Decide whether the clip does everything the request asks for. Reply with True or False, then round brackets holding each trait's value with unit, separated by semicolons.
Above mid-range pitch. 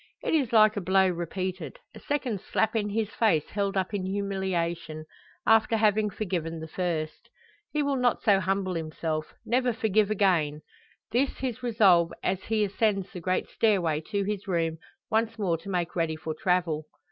True (195 Hz)